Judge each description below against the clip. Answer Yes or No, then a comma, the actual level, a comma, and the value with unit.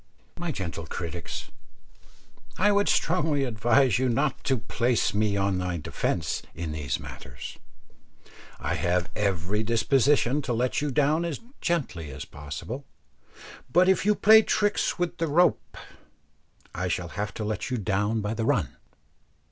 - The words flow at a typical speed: Yes, average, 150 wpm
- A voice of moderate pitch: No, low, 115 Hz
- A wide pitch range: Yes, wide, 8.2 semitones